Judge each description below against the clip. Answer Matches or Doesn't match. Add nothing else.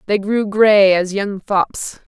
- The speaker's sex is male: Doesn't match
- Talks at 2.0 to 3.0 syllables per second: Doesn't match